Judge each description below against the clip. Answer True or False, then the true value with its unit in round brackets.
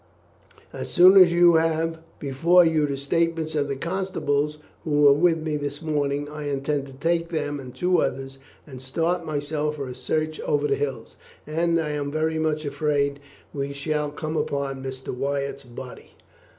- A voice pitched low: False (150 Hz)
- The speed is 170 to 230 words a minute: True (175 wpm)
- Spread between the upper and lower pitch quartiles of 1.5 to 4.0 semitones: True (2.4 semitones)